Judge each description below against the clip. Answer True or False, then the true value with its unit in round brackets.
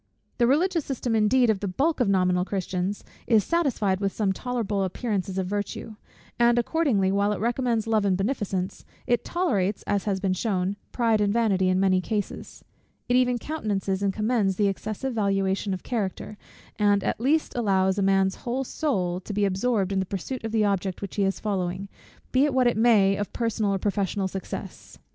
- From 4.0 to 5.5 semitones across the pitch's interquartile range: False (3.6 semitones)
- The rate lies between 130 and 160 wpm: False (190 wpm)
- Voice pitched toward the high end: True (205 Hz)